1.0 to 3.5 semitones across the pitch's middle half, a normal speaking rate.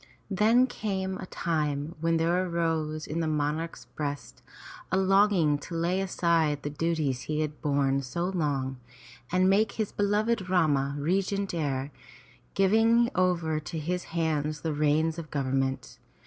No: average, 4.1 semitones; average, 145 wpm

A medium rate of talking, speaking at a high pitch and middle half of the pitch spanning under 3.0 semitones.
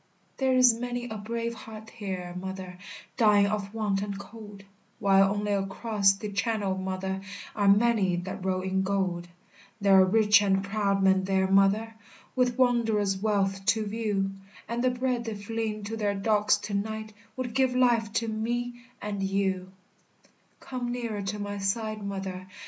Yes: average, 160 wpm; high, 205 Hz; narrow, 2.5 semitones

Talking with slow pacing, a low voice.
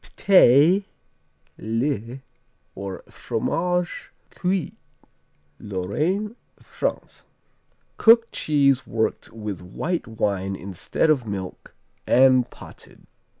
Yes: slow, 80 wpm; low, 130 Hz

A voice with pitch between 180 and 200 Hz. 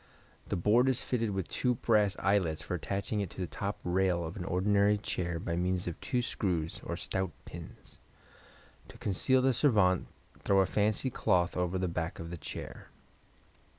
No: very low, 95 Hz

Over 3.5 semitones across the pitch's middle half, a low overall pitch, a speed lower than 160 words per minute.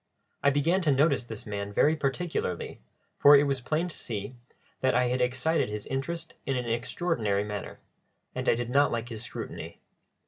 No: average, 4.4 semitones; low, 130 Hz; average, 180 wpm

